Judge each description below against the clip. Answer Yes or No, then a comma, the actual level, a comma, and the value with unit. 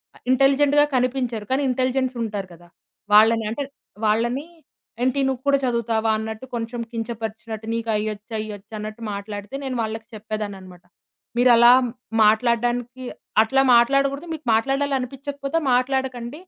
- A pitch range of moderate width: Yes, average, 3.3 semitones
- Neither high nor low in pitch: No, high, 235 Hz